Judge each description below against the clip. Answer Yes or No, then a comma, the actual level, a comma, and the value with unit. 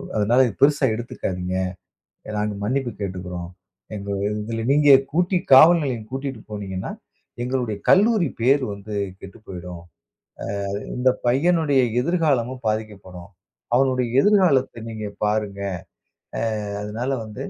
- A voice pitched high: No, low, 115 Hz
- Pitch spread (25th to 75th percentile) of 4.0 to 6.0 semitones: Yes, average, 4.8 semitones